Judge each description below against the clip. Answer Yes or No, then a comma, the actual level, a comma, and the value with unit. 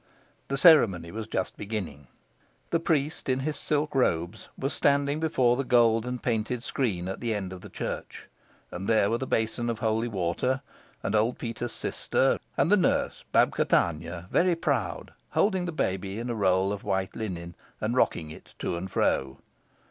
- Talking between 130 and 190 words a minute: Yes, average, 180 wpm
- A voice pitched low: Yes, low, 115 Hz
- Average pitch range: No, wide, 5.8 semitones